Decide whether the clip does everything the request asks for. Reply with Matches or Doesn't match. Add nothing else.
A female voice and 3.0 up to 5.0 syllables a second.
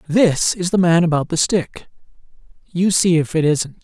Doesn't match